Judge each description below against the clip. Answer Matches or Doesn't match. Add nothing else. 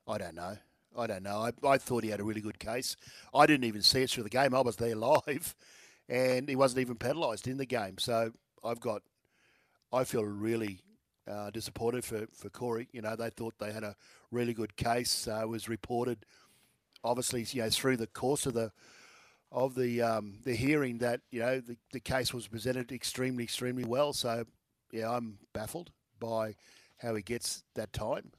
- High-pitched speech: Doesn't match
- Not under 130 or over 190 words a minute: Doesn't match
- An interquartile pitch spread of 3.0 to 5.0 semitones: Doesn't match